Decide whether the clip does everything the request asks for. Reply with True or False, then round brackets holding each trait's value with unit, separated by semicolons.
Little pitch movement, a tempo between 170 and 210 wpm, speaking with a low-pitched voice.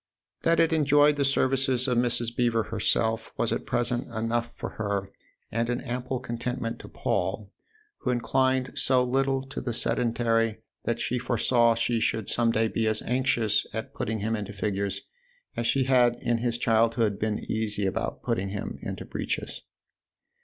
True (2.3 semitones; 175 wpm; 120 Hz)